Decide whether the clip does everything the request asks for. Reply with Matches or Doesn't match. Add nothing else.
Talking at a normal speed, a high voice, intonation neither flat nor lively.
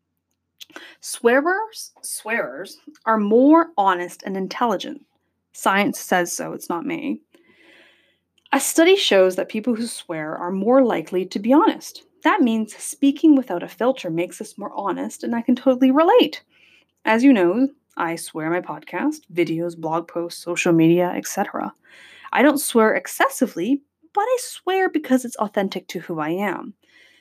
Doesn't match